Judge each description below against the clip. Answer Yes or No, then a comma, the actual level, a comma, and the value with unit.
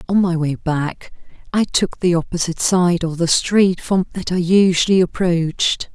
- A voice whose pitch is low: No, medium, 175 Hz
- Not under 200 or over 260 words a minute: No, average, 170 wpm